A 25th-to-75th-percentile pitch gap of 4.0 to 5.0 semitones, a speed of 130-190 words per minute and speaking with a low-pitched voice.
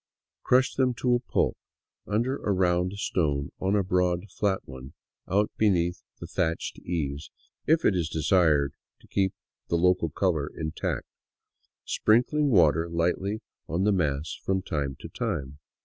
Yes: average, 4.5 semitones; average, 155 wpm; very low, 90 Hz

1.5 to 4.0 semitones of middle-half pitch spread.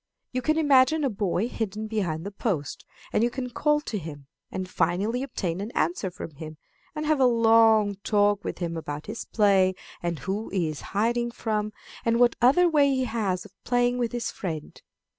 No: average, 4.8 semitones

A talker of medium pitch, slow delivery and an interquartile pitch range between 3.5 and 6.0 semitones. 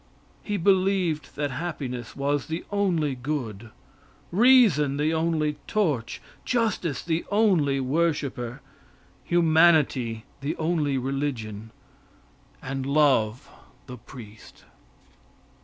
Yes: medium, 145 Hz; slow, 90 wpm; average, 4.6 semitones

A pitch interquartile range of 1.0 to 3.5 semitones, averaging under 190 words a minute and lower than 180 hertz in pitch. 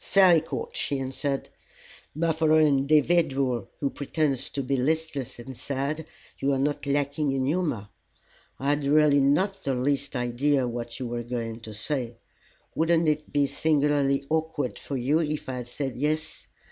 Yes: average, 2.8 semitones; average, 160 wpm; medium, 140 Hz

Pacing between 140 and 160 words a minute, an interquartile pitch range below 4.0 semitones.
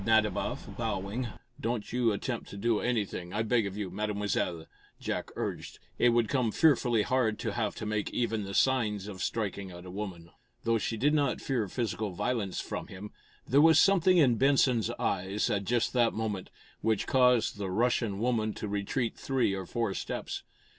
No: average, 180 wpm; average, 3.5 semitones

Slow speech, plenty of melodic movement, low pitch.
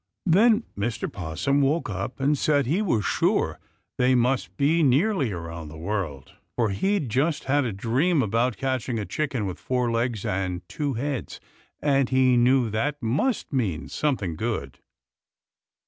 No: average, 155 wpm; wide, 5.8 semitones; low, 125 Hz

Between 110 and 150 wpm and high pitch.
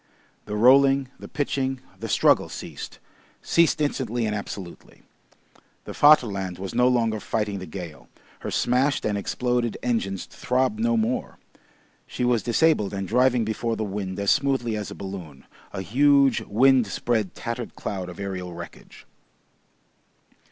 No: average, 140 wpm; low, 115 Hz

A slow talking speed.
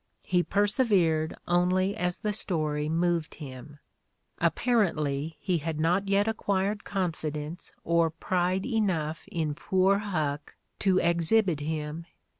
Yes: slow, 115 wpm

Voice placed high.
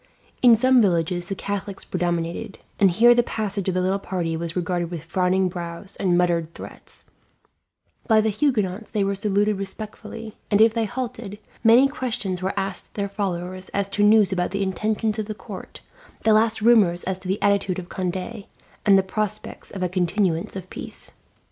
Yes: high, 195 Hz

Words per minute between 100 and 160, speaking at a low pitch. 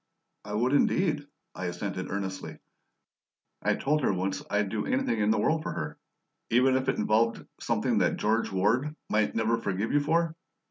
No: average, 175 wpm; low, 110 Hz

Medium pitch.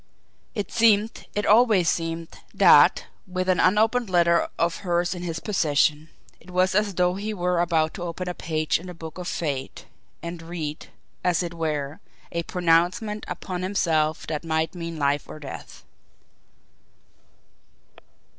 Yes: medium, 175 Hz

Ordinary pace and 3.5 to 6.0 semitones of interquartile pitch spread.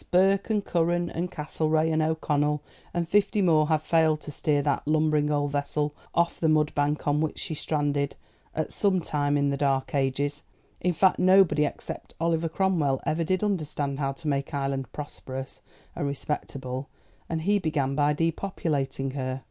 No: average, 165 wpm; narrow, 2.6 semitones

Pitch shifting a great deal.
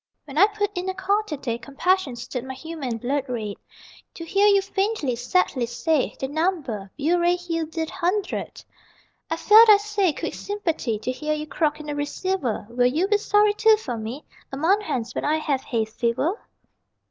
Yes: wide, 7.1 semitones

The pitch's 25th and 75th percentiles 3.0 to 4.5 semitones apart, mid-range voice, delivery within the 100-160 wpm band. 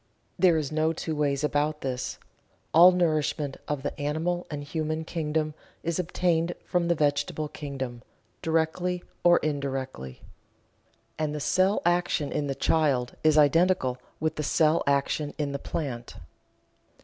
No: narrow, 2.5 semitones; medium, 155 Hz; average, 140 wpm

